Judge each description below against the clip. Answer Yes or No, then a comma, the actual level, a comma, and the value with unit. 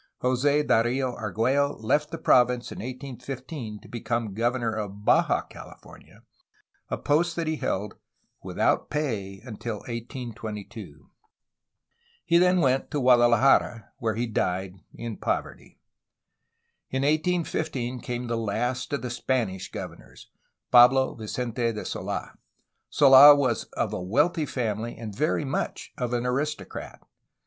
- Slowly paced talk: Yes, slow, 125 wpm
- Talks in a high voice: No, low, 125 Hz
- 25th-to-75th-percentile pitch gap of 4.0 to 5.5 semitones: No, average, 3.5 semitones